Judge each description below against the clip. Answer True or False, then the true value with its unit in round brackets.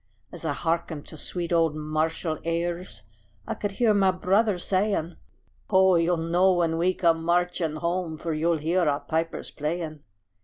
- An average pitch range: False (2.1 semitones)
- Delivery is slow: False (160 wpm)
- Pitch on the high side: False (170 Hz)